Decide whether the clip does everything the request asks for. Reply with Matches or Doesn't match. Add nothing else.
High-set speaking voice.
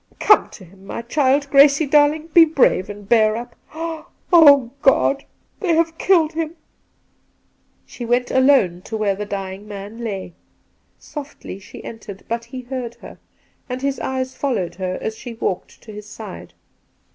Matches